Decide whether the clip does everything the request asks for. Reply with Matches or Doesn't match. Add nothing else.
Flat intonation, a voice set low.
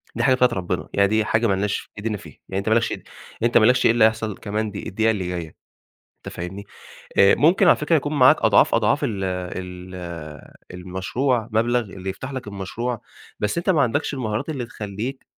Doesn't match